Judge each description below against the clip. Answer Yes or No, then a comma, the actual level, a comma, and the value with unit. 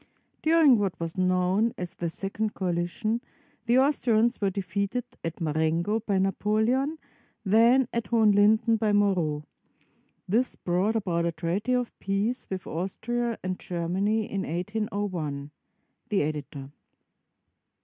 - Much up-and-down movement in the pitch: No, average, 4.3 semitones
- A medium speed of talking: No, slow, 130 wpm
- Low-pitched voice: No, high, 200 Hz